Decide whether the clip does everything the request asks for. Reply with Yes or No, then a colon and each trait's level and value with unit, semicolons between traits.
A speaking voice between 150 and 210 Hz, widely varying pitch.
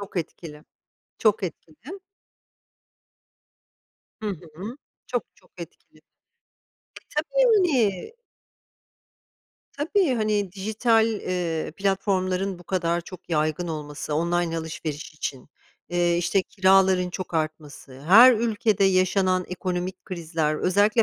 No: medium, 185 Hz; average, 3.7 semitones